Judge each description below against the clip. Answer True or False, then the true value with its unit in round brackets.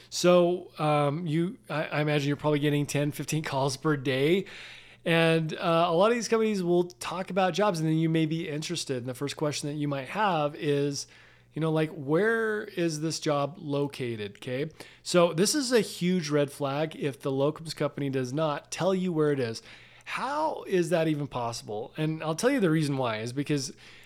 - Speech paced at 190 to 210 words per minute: True (200 wpm)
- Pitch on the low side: False (155 Hz)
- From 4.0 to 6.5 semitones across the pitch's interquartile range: False (3.4 semitones)